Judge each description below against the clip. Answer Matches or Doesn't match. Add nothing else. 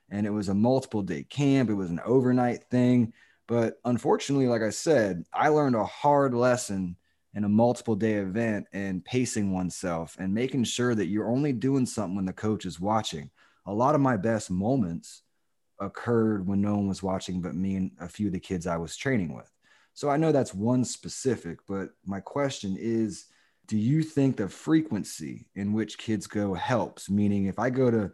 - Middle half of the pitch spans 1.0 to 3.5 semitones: Doesn't match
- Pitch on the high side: Doesn't match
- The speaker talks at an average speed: Matches